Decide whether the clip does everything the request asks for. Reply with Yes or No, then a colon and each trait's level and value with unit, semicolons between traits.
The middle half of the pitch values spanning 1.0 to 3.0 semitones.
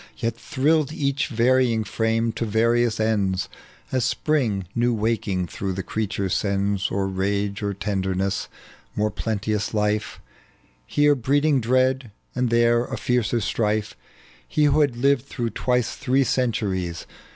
No: average, 3.8 semitones